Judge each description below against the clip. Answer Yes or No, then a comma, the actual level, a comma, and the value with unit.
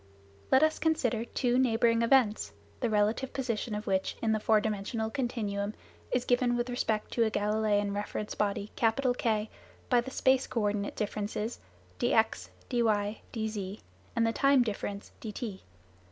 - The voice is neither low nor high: No, high, 220 Hz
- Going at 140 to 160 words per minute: Yes, average, 150 wpm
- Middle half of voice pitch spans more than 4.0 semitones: No, average, 2.7 semitones